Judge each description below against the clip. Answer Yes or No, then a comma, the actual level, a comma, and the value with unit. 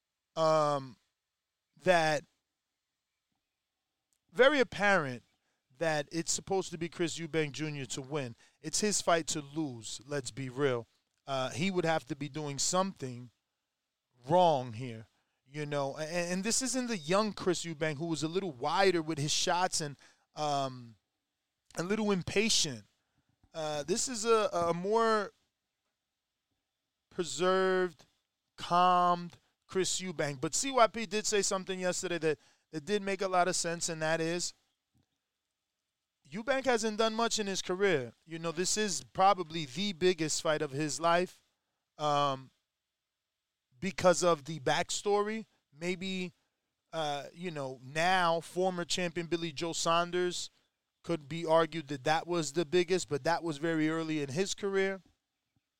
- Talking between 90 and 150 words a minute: Yes, average, 140 wpm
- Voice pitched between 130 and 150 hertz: No, medium, 170 Hz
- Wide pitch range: No, average, 3.8 semitones